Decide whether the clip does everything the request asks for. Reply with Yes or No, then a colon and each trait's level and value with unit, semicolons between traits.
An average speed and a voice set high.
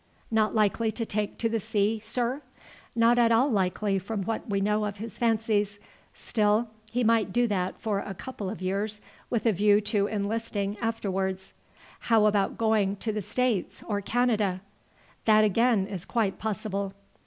Yes: average, 165 wpm; high, 215 Hz